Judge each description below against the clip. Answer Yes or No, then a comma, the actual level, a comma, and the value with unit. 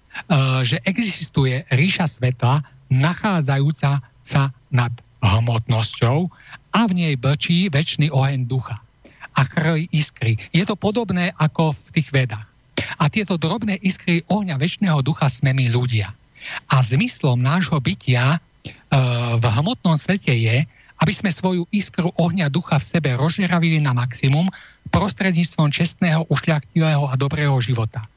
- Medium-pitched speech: Yes, medium, 150 Hz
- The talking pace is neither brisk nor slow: Yes, average, 130 wpm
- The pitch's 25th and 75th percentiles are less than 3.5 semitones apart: No, average, 5.0 semitones